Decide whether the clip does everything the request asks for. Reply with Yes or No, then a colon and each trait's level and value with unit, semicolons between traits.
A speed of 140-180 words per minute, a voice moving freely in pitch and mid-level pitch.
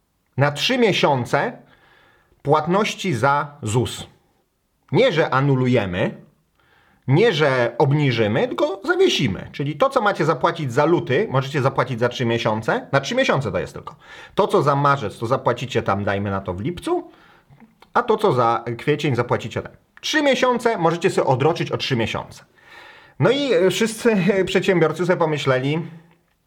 Yes: average, 145 wpm; wide, 7.7 semitones; medium, 150 Hz